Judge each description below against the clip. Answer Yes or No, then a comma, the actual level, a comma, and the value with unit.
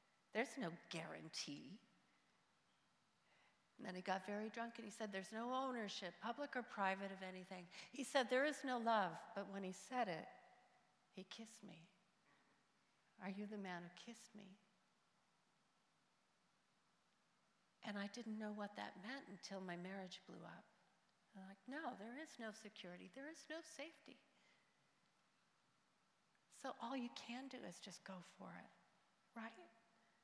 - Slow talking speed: No, average, 150 wpm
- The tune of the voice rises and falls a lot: No, average, 4.0 semitones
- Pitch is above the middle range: Yes, high, 210 Hz